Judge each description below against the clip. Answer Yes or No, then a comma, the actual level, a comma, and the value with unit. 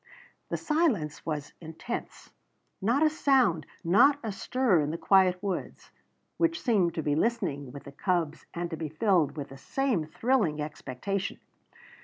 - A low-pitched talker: No, medium, 180 Hz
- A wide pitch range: Yes, wide, 7.5 semitones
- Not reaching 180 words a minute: Yes, average, 155 wpm